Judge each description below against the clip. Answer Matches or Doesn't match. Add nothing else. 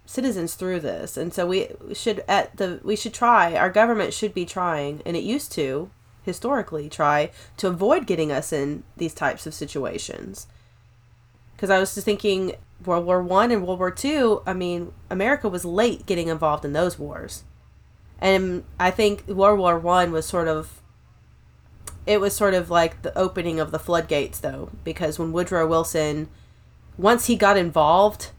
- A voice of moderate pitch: Matches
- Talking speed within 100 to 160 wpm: Doesn't match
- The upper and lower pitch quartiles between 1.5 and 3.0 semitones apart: Doesn't match